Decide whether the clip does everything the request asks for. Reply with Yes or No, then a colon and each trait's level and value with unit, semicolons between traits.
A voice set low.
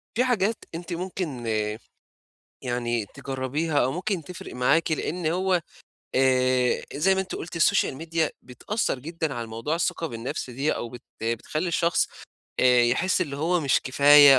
No: medium, 150 Hz